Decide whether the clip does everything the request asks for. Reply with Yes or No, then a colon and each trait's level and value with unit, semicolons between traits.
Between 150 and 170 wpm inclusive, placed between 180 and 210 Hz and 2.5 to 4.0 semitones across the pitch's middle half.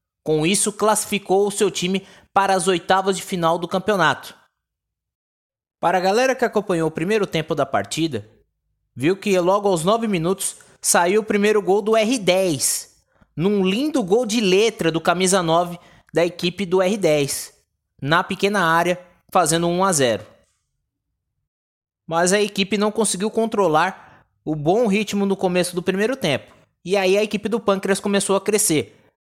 Yes: average, 155 wpm; high, 190 Hz; average, 3.4 semitones